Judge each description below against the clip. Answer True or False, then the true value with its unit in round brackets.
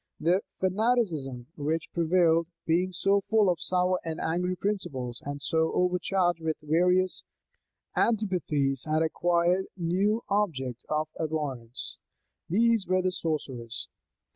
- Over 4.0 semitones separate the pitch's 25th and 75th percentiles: False (3.3 semitones)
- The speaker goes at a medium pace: False (120 wpm)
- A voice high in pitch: False (170 Hz)